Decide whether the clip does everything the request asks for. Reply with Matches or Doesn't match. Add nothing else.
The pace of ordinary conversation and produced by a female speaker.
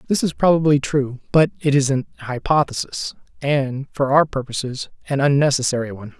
Doesn't match